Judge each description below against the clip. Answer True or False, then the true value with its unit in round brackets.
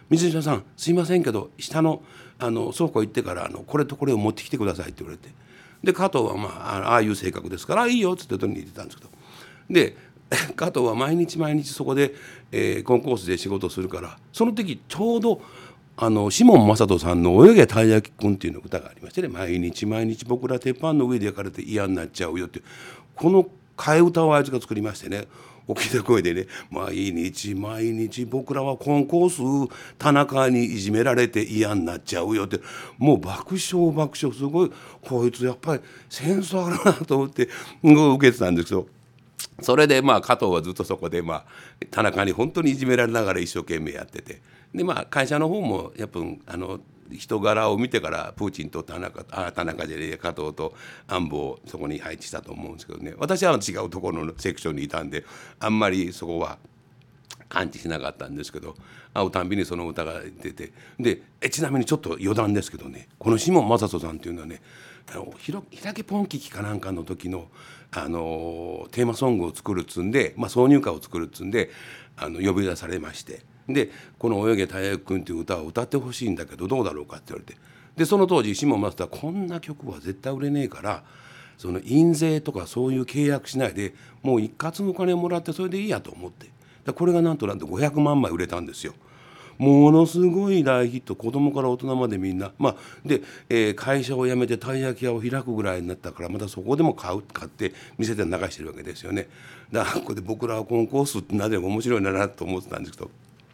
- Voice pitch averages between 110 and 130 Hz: True (125 Hz)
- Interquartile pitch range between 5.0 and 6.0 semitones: False (6.6 semitones)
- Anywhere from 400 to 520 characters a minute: True (405 characters per minute)